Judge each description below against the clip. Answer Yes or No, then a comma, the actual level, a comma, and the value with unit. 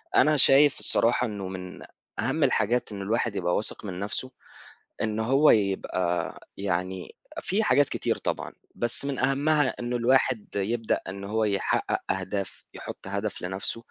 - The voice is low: Yes, low, 110 Hz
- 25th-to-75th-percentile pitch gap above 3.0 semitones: Yes, average, 4.8 semitones